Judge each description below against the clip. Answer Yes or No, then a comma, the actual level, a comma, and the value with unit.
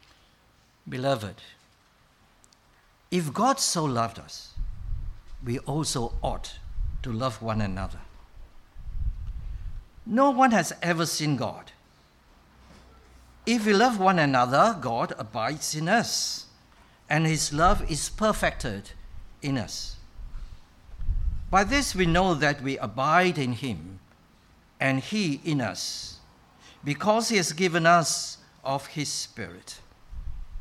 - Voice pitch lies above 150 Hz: No, low, 135 Hz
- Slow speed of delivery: Yes, slow, 110 wpm